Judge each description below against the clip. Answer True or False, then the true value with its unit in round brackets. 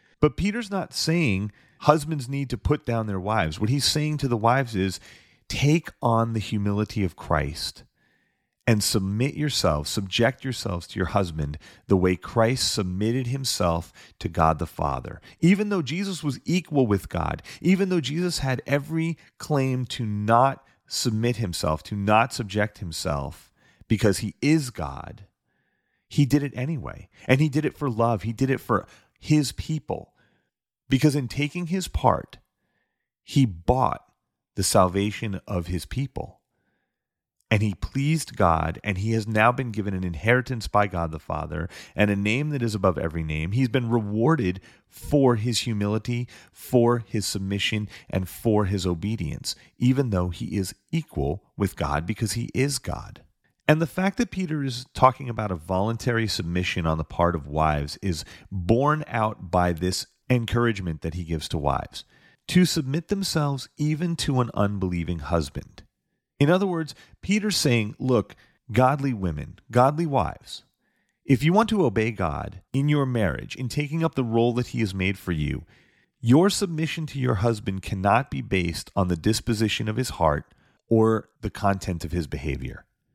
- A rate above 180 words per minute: False (165 wpm)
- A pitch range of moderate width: False (6.6 semitones)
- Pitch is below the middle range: True (115 Hz)